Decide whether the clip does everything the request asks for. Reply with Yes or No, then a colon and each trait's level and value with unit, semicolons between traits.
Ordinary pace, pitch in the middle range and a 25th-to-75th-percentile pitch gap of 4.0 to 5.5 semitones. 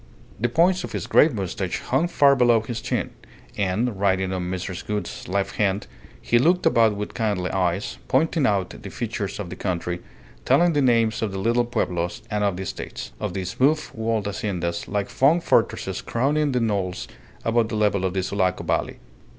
No: average, 185 wpm; low, 105 Hz; average, 4.4 semitones